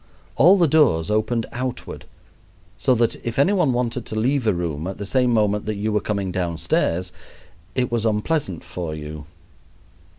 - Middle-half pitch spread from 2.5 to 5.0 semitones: No, wide, 5.5 semitones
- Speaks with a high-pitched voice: No, low, 110 Hz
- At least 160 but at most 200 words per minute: Yes, average, 170 wpm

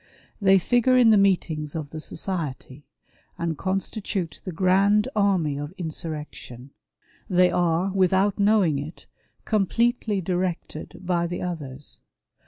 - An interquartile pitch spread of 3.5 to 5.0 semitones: Yes, average, 3.9 semitones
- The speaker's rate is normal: No, slow, 120 wpm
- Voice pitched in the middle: Yes, medium, 180 Hz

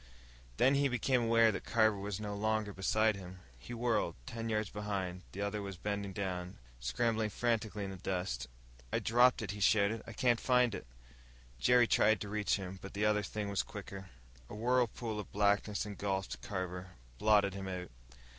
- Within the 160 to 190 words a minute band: Yes, average, 180 wpm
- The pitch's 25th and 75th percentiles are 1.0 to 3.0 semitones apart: Yes, narrow, 2.6 semitones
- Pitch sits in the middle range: No, low, 105 Hz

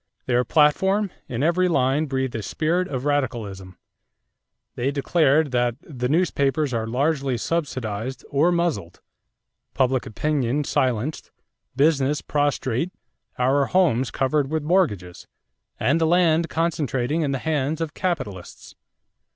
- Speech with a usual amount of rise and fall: Yes, average, 4.2 semitones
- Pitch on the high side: No, medium, 140 Hz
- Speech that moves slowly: Yes, slow, 120 wpm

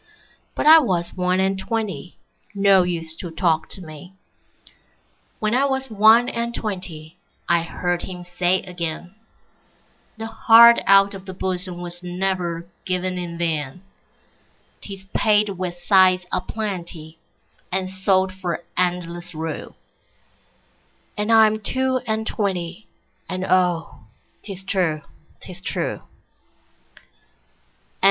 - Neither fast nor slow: No, slow, 100 wpm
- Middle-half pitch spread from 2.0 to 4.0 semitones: Yes, average, 2.7 semitones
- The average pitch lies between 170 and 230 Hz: Yes, medium, 185 Hz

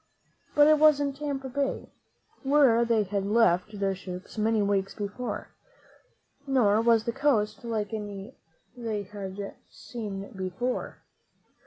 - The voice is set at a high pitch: Yes, high, 220 Hz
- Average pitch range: Yes, average, 4.2 semitones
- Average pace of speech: No, slow, 130 wpm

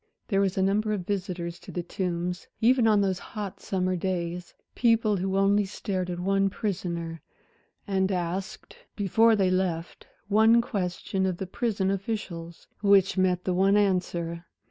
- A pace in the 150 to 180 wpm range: Yes, average, 155 wpm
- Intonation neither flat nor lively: No, narrow, 2.3 semitones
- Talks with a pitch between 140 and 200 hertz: Yes, high, 190 Hz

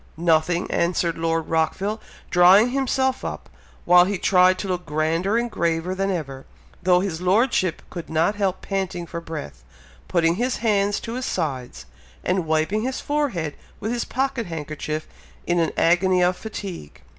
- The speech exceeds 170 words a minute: No, average, 155 wpm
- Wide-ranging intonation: No, average, 3.8 semitones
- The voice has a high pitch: No, medium, 180 Hz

